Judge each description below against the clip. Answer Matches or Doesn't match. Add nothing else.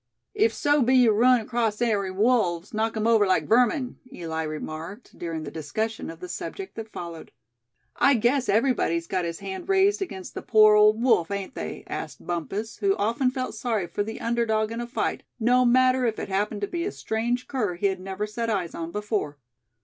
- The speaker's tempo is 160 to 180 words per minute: Doesn't match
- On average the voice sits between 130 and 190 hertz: Doesn't match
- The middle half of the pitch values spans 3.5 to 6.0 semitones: Matches